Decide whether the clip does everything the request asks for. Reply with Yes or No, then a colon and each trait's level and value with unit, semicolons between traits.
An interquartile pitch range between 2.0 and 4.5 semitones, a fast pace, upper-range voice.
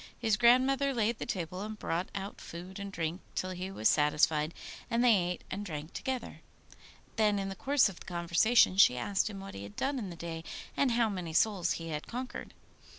No: average, 5.0 semitones; fast, 210 wpm; high, 195 Hz